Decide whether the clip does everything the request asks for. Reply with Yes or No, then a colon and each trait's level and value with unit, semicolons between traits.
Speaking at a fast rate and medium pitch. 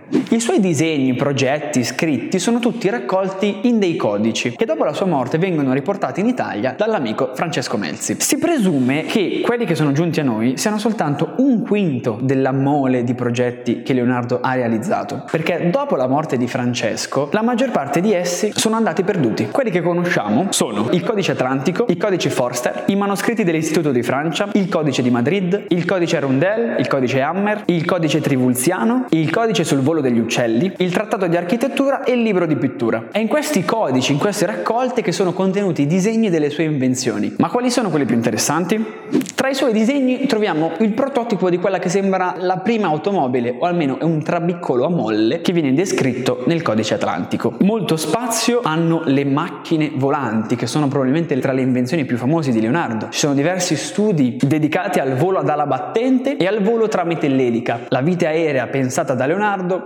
Yes: fast, 185 wpm; medium, 170 Hz